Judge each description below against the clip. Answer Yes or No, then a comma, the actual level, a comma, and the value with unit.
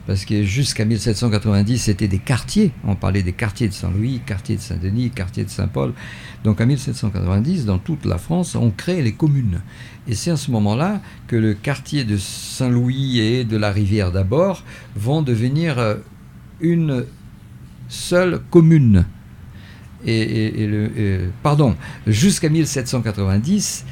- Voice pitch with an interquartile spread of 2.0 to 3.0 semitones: No, average, 4.6 semitones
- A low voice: Yes, low, 110 Hz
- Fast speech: No, slow, 145 wpm